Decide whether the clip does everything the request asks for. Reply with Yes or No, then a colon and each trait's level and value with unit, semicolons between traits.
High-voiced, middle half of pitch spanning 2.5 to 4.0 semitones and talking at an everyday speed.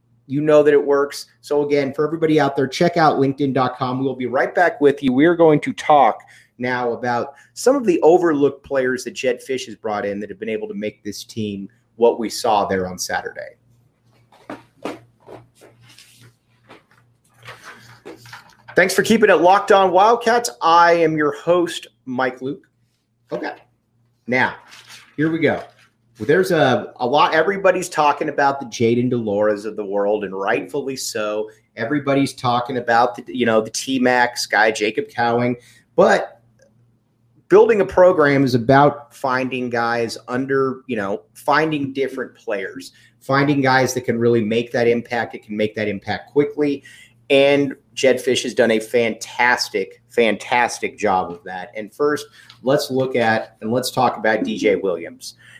No: low, 125 Hz; average, 3.6 semitones; average, 160 wpm